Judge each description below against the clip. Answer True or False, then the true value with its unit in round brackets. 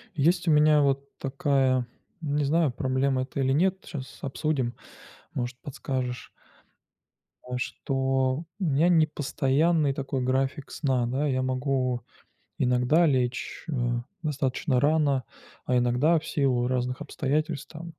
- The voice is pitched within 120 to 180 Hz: True (135 Hz)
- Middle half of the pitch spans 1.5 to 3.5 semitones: True (2.8 semitones)